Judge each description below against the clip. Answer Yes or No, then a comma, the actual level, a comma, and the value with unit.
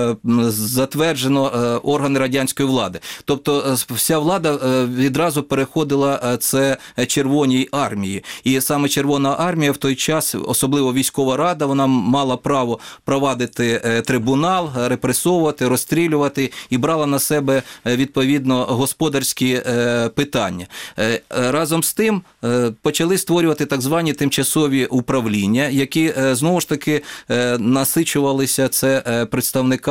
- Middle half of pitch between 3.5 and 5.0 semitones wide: No, narrow, 2.6 semitones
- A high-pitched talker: No, low, 135 Hz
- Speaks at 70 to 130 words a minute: Yes, slow, 105 wpm